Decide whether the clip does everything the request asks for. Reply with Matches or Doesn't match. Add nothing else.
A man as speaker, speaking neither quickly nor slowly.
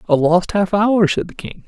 Doesn't match